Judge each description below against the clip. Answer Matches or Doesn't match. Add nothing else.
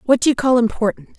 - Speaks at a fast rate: Matches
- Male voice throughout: Doesn't match